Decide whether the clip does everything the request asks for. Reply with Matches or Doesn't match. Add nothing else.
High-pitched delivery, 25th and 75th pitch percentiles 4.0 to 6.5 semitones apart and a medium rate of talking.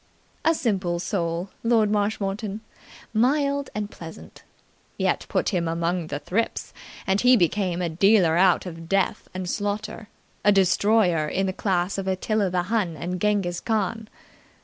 Doesn't match